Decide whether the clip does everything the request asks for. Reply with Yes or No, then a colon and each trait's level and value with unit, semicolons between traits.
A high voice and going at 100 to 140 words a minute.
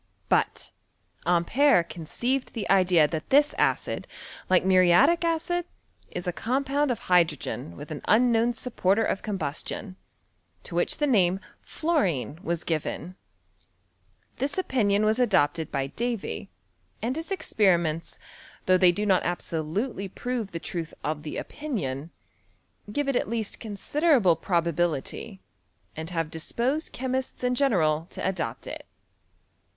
Yes: high, 195 Hz; slow, 135 wpm